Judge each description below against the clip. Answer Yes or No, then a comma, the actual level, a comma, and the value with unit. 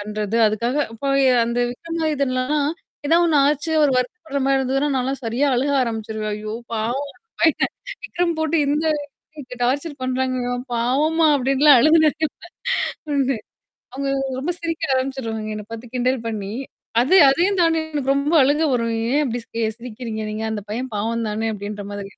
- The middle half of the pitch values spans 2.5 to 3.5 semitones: No, average, 4.3 semitones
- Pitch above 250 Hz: Yes, very high, 260 Hz